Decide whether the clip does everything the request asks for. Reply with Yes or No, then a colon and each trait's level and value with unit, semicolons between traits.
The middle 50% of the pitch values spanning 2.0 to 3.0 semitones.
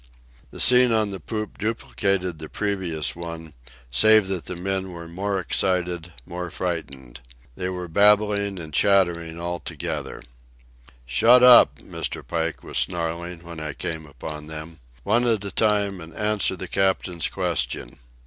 No: average, 3.6 semitones